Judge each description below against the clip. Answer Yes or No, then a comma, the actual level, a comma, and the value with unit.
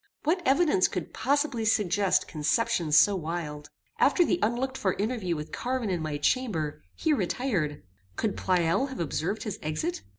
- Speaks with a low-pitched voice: No, high, 195 Hz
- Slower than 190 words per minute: Yes, average, 155 wpm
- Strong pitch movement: Yes, wide, 7.8 semitones